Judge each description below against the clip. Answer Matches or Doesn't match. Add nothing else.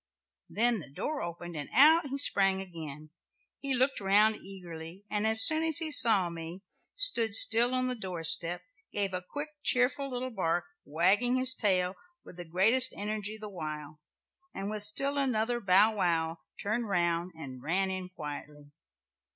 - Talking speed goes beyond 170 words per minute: Doesn't match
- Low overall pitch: Doesn't match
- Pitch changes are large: Matches